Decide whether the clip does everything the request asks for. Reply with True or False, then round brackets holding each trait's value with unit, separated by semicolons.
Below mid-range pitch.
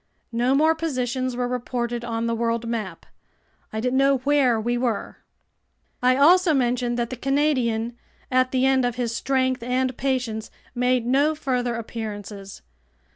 False (250 Hz)